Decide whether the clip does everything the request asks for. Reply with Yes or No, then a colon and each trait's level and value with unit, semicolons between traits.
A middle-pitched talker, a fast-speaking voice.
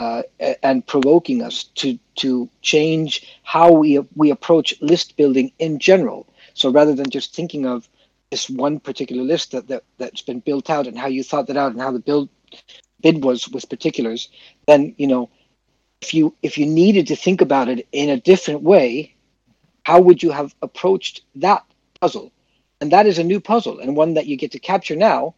No: medium, 150 Hz; average, 195 wpm